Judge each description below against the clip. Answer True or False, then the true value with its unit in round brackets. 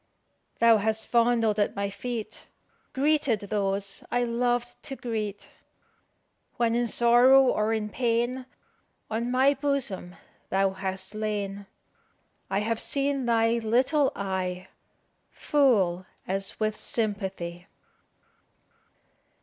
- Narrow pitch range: False (3.6 semitones)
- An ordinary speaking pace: False (110 wpm)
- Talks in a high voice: True (225 Hz)